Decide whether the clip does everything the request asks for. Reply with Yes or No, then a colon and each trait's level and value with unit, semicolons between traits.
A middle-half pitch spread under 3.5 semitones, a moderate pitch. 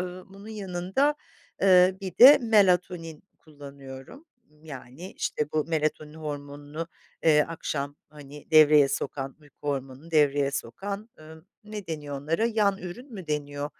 No: average, 4.5 semitones; medium, 155 Hz